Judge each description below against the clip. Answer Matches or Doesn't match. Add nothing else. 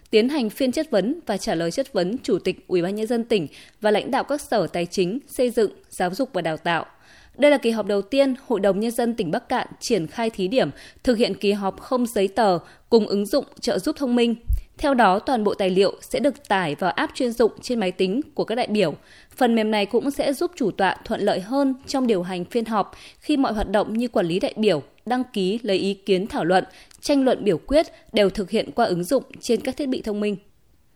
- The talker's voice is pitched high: Matches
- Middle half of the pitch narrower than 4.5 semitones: Doesn't match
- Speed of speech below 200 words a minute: Doesn't match